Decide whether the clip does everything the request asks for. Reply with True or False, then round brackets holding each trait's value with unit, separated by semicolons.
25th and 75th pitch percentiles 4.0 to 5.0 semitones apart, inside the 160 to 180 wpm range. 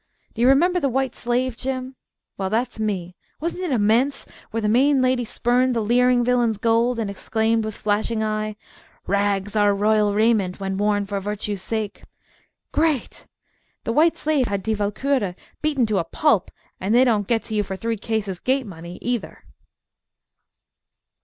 False (3.5 semitones; 165 wpm)